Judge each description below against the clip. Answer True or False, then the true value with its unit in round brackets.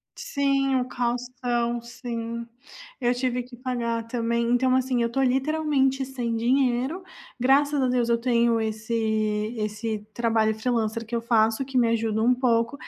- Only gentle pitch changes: True (2.0 semitones)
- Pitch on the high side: True (240 Hz)